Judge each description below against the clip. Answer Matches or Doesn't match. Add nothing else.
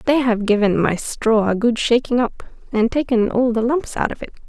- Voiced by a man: Doesn't match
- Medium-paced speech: Doesn't match